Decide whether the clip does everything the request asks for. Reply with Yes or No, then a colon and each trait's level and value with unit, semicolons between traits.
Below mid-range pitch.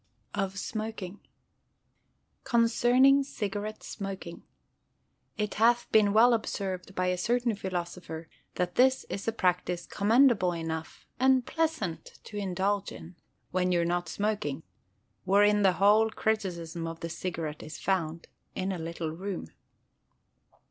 No: high, 195 Hz